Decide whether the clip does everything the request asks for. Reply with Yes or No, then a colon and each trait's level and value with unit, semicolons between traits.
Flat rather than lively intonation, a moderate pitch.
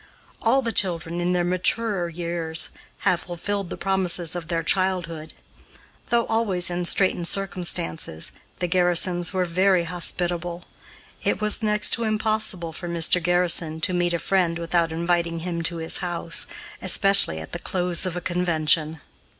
Yes: narrow, 1.9 semitones; medium, 175 Hz